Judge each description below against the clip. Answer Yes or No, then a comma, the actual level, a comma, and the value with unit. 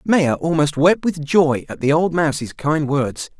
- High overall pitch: No, medium, 155 Hz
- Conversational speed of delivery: Yes, average, 195 wpm